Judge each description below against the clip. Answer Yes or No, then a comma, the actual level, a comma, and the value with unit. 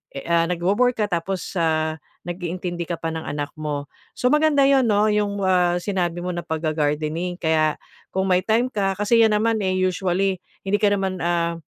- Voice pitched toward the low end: No, medium, 180 Hz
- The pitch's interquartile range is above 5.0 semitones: No, average, 3.6 semitones